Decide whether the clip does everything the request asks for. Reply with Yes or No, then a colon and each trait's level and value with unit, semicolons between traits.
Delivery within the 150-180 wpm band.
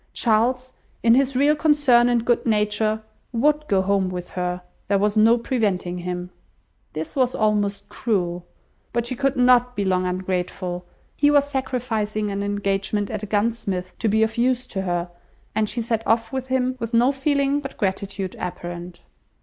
Yes: average, 170 wpm